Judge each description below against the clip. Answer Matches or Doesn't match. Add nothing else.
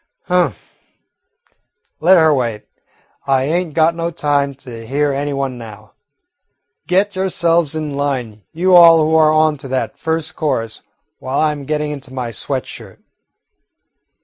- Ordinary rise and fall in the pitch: Matches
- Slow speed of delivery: Doesn't match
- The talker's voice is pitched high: Doesn't match